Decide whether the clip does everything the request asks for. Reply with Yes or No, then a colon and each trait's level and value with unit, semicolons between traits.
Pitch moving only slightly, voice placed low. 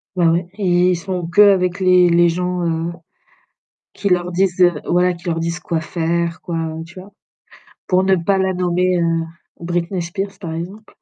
No: narrow, 1.4 semitones; medium, 175 Hz